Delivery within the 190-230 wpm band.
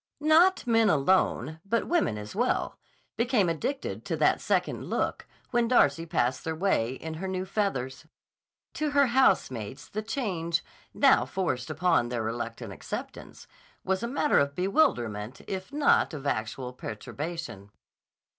No: average, 140 wpm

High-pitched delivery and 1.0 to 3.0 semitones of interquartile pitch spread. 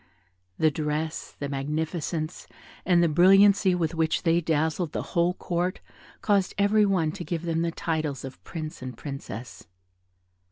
No: medium, 165 Hz; narrow, 2.5 semitones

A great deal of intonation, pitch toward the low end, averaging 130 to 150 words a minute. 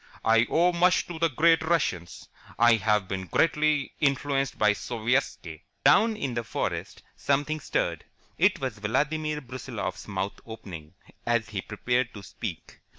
Yes: wide, 6.4 semitones; low, 125 Hz; average, 145 wpm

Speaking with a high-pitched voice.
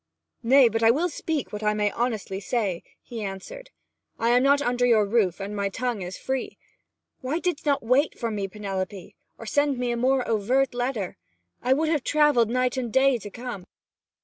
Yes: high, 240 Hz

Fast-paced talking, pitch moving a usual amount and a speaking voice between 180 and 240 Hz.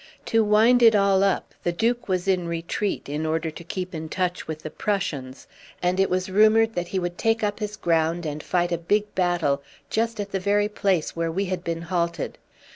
Yes: fast, 210 wpm; average, 3.6 semitones; medium, 185 Hz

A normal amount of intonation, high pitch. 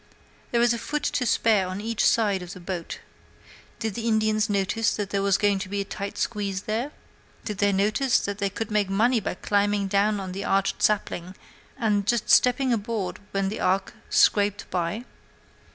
No: narrow, 2.3 semitones; high, 205 Hz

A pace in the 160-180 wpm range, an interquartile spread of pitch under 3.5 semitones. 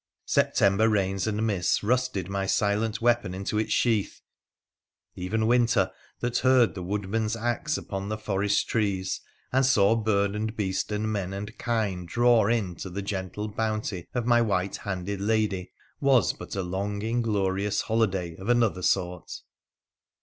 No: average, 150 wpm; narrow, 2.6 semitones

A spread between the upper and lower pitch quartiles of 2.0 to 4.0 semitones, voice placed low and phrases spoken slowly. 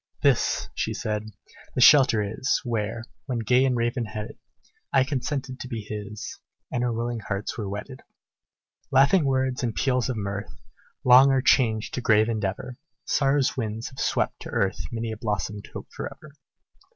No: average, 3.5 semitones; low, 120 Hz; average, 165 wpm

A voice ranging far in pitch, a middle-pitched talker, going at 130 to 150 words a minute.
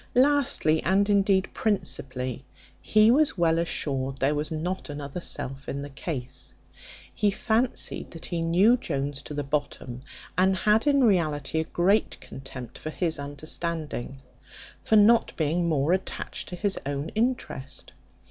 Yes: wide, 6.0 semitones; medium, 165 Hz; average, 145 wpm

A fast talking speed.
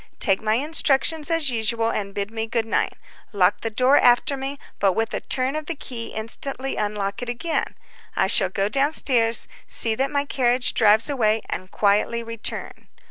No: average, 185 wpm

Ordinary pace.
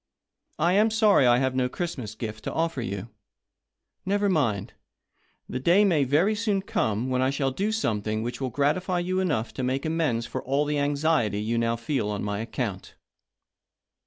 Yes: average, 190 wpm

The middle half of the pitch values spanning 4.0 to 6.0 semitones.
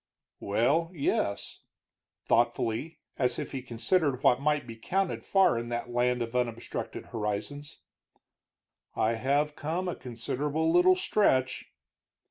Yes: average, 4.7 semitones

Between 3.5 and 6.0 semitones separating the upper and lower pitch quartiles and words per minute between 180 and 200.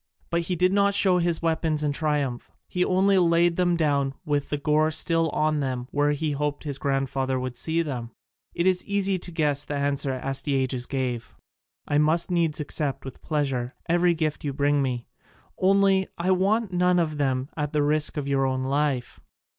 Yes: average, 3.8 semitones; average, 185 wpm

